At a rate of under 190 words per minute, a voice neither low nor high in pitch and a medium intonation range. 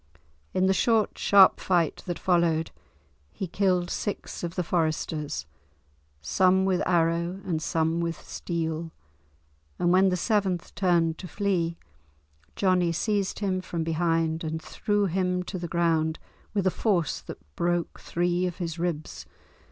No: average, 145 wpm; medium, 175 Hz; narrow, 2.2 semitones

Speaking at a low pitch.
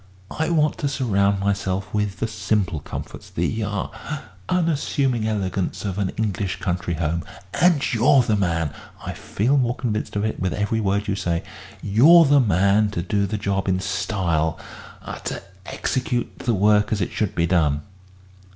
Yes: low, 100 Hz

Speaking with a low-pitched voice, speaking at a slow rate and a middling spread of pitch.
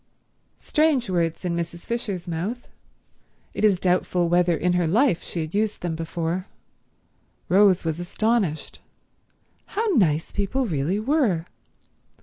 No: medium, 180 Hz; slow, 130 wpm; average, 4.3 semitones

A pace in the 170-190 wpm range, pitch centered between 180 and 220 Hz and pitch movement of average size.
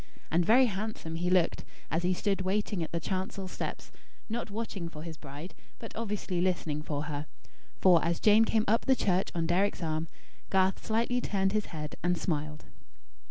Yes: average, 180 wpm; medium, 185 Hz; average, 4.2 semitones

